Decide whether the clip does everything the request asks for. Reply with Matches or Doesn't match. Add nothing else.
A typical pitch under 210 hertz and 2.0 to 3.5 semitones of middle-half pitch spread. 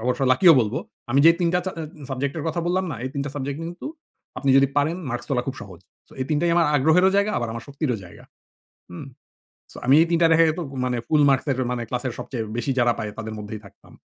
Doesn't match